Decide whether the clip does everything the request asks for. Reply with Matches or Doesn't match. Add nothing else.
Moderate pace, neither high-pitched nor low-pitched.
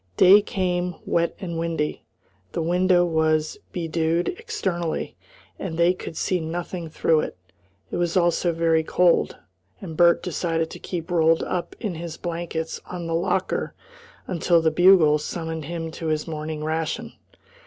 Matches